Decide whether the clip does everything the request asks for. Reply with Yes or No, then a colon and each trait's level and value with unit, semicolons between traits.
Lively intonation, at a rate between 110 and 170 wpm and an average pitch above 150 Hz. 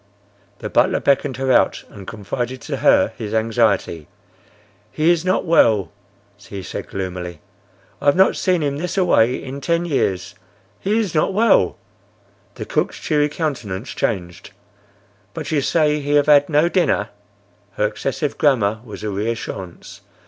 No: wide, 6.6 semitones; average, 155 wpm; low, 135 Hz